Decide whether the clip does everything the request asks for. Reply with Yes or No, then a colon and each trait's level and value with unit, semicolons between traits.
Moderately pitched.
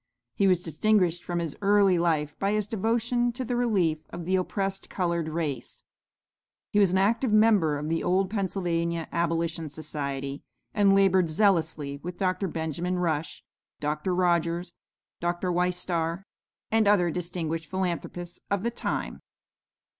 Yes: medium, 175 Hz